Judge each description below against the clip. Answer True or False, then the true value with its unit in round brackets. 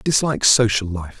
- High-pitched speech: False (110 Hz)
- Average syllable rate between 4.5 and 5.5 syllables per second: True (5.3 syllables/s)